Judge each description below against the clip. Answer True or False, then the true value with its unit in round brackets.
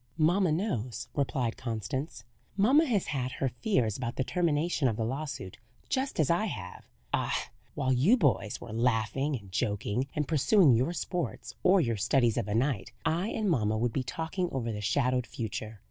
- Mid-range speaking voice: False (130 Hz)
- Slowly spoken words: False (175 wpm)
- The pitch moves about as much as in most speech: False (6.6 semitones)